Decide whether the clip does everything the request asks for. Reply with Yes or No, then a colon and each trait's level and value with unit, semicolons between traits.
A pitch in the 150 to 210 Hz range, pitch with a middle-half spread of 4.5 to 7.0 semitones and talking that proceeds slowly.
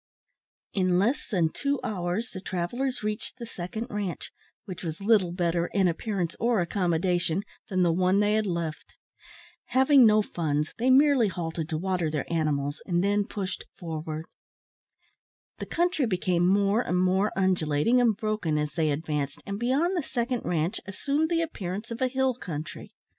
No: high, 190 Hz; average, 5.2 semitones; average, 165 wpm